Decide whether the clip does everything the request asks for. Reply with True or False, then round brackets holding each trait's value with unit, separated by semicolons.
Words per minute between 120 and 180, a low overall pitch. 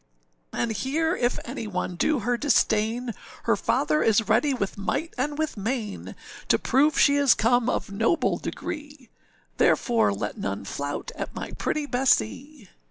False (155 wpm; 245 Hz)